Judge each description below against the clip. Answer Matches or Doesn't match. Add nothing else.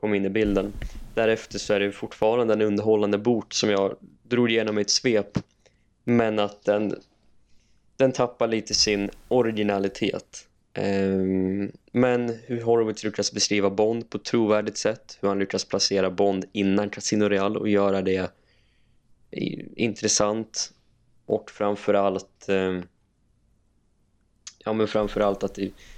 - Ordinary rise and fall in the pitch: Doesn't match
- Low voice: Matches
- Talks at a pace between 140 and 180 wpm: Doesn't match